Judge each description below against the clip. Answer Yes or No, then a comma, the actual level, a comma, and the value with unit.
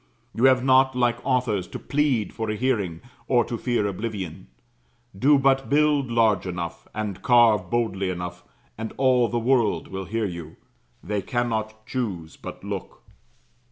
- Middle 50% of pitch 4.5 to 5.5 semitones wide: Yes, average, 4.8 semitones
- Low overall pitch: Yes, low, 115 Hz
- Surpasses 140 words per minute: Yes, average, 155 wpm